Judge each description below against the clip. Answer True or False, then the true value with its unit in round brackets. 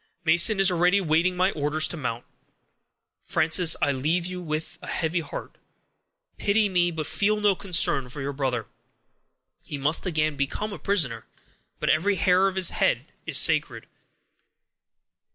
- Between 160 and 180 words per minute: False (150 wpm)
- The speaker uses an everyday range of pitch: True (4.1 semitones)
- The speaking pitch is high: False (170 Hz)